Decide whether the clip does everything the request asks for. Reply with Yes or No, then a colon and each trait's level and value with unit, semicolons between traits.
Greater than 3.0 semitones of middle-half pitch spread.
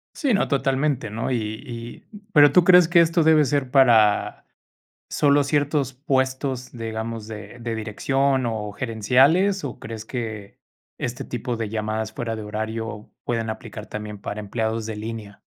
Yes: average, 4.0 semitones